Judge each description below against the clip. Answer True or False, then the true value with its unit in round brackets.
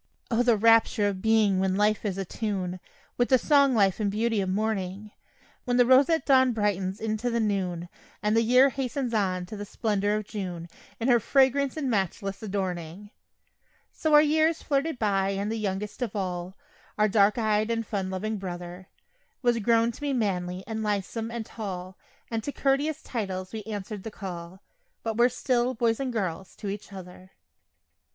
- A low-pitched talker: False (215 Hz)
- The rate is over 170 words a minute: True (180 wpm)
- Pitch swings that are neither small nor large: True (3.7 semitones)